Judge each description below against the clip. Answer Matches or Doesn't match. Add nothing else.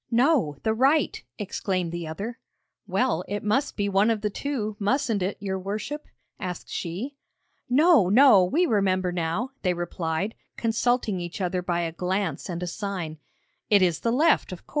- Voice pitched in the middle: Doesn't match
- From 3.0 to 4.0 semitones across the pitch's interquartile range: Doesn't match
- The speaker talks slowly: Doesn't match